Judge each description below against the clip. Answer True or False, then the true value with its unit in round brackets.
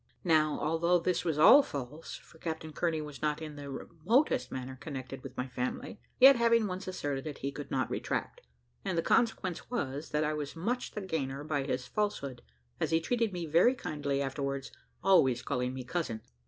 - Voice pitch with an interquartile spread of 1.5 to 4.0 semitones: False (4.6 semitones)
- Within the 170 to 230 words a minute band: True (190 wpm)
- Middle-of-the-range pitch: True (150 Hz)